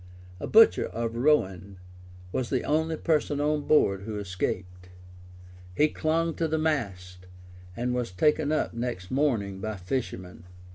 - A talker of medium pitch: No, low, 120 Hz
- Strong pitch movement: Yes, wide, 7.9 semitones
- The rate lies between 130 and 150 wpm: Yes, average, 140 wpm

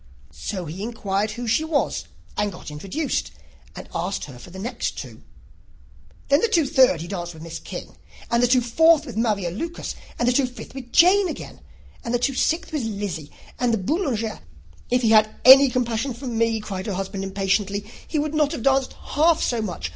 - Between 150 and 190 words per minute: No, fast, 205 wpm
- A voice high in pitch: Yes, high, 230 Hz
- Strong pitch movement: Yes, wide, 5.7 semitones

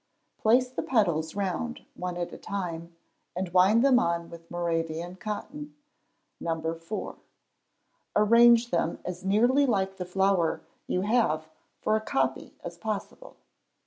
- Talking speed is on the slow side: Yes, slow, 130 wpm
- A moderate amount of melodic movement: Yes, average, 4.7 semitones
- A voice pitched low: No, high, 190 Hz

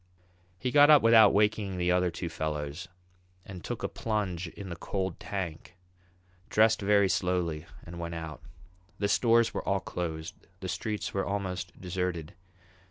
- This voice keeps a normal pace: Yes, average, 155 wpm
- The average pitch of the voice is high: No, very low, 90 Hz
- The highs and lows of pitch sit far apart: No, average, 3.4 semitones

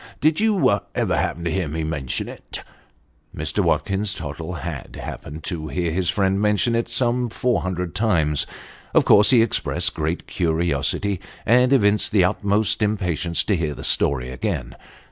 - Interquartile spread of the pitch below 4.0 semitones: No, average, 5.1 semitones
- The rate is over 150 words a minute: Yes, average, 165 wpm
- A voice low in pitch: Yes, very low, 90 Hz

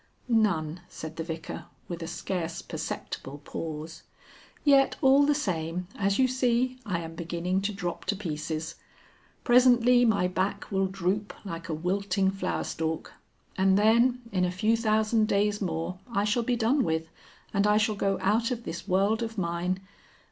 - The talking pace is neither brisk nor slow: Yes, average, 160 wpm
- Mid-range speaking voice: No, high, 195 Hz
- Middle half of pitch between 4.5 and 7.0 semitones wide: Yes, average, 4.8 semitones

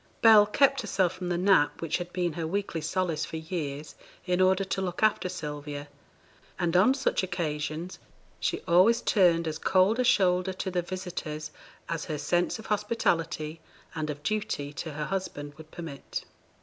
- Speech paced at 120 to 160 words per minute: No, average, 170 wpm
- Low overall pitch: No, medium, 175 Hz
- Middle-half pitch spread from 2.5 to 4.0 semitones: Yes, average, 3.4 semitones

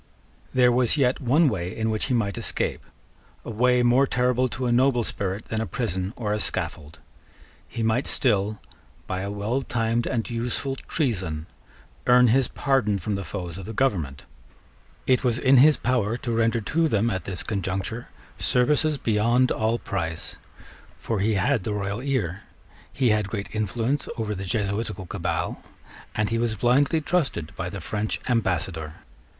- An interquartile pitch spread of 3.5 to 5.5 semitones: Yes, average, 3.9 semitones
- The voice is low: Yes, low, 115 Hz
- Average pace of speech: Yes, average, 165 wpm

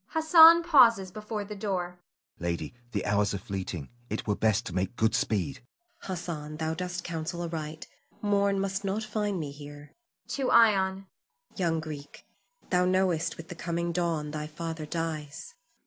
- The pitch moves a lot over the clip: No, average, 4.7 semitones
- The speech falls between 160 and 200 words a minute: Yes, average, 165 wpm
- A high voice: No, medium, 170 Hz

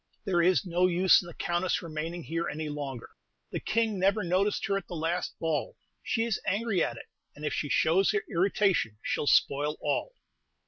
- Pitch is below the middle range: No, medium, 175 Hz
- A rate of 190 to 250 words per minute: Yes, average, 195 wpm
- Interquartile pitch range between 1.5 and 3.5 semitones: No, average, 4.0 semitones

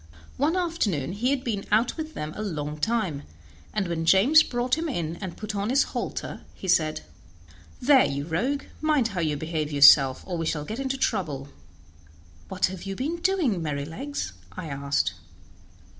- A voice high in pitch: Yes, high, 195 Hz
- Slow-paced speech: No, average, 175 wpm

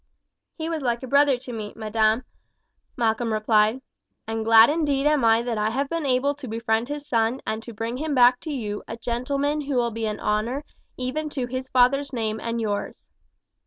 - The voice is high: Yes, high, 245 Hz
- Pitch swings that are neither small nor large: Yes, average, 3.8 semitones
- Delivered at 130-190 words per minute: No, average, 200 wpm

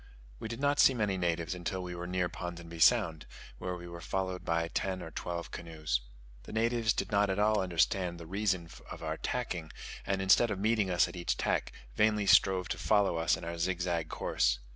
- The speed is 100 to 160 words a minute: No, fast, 205 wpm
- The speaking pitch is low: Yes, very low, 90 Hz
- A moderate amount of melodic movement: Yes, average, 3.2 semitones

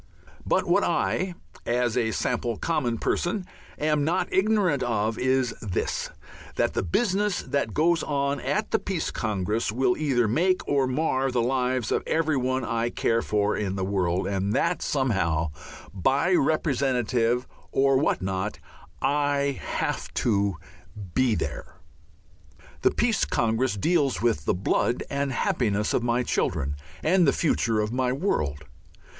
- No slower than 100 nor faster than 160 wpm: Yes, average, 145 wpm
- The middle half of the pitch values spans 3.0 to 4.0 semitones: No, average, 5.2 semitones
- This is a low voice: Yes, low, 125 Hz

